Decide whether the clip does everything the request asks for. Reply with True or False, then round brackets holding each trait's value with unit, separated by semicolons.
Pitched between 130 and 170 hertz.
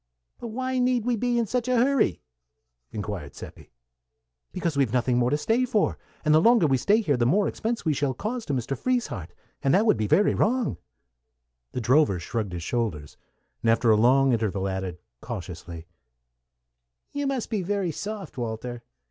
True (140 Hz)